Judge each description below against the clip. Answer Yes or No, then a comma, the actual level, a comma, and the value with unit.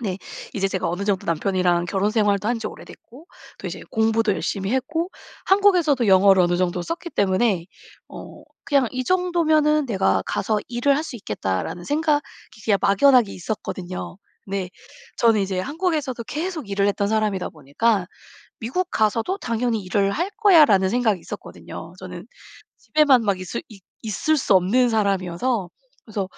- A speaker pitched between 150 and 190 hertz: No, high, 220 Hz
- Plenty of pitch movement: Yes, wide, 6.4 semitones